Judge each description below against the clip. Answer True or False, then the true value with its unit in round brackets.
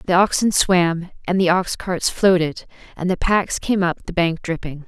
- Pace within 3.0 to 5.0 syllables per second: True (4.5 syllables/s)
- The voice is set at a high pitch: False (180 Hz)